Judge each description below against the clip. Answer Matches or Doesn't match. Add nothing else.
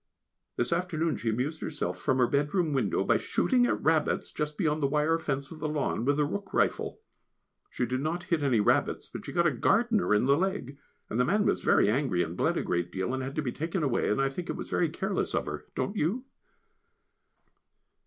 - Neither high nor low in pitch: Matches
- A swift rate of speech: Matches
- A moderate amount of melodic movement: Matches